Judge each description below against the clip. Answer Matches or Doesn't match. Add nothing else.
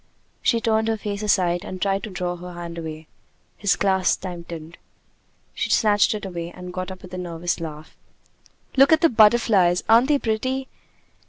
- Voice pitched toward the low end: Doesn't match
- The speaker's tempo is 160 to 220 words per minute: Matches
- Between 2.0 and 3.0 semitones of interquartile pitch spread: Doesn't match